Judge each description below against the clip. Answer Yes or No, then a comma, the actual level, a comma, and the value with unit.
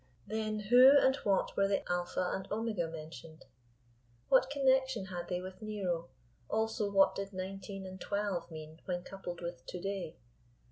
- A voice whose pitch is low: No, high, 195 Hz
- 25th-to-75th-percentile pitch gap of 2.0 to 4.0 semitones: Yes, average, 3.3 semitones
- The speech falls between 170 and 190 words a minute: No, average, 155 wpm